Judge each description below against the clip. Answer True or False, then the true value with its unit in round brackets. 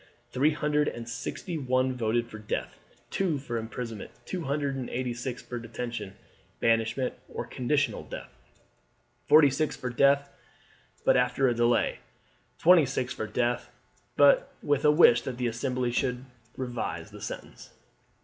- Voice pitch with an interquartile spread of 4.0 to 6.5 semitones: False (3.0 semitones)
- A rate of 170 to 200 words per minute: False (150 wpm)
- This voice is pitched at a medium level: False (125 Hz)